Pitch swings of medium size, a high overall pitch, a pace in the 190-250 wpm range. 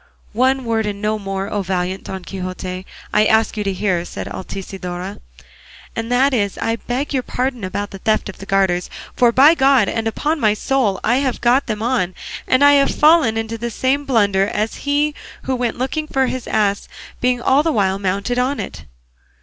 Yes: average, 4.9 semitones; high, 225 Hz; fast, 205 wpm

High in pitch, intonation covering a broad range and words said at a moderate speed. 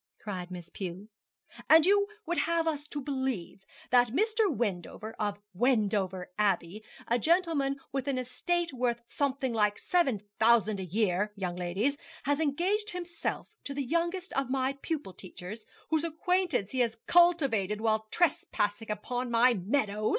Yes: very high, 250 Hz; wide, 7.2 semitones; average, 150 wpm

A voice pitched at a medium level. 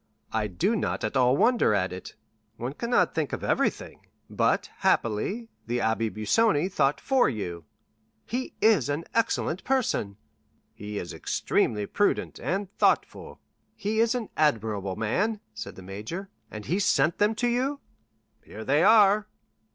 Yes: medium, 150 Hz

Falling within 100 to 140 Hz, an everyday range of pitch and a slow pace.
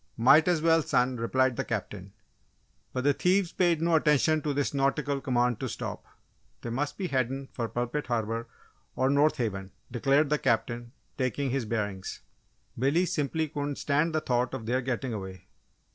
No: low, 135 Hz; average, 4.0 semitones; average, 170 wpm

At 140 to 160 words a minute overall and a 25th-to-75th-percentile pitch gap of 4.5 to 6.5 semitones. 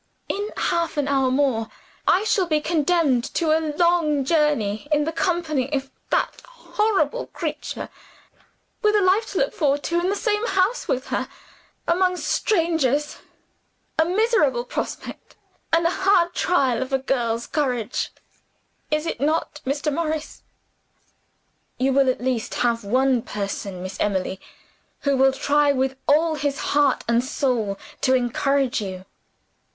Yes: average, 145 wpm; average, 4.8 semitones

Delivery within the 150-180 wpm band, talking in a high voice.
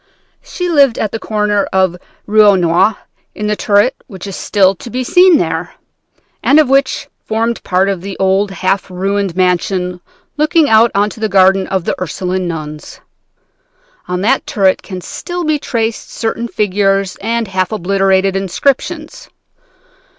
Yes: average, 155 wpm; high, 200 Hz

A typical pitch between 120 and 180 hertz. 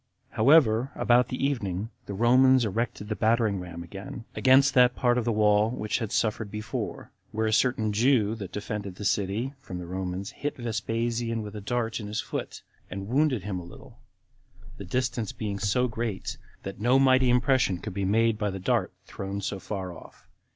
No: low, 110 Hz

